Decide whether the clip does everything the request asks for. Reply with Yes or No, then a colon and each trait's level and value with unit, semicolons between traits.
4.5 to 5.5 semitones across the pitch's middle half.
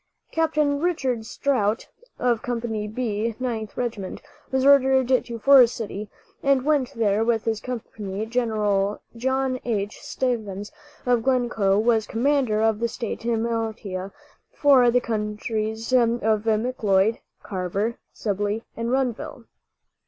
No: average, 3.0 semitones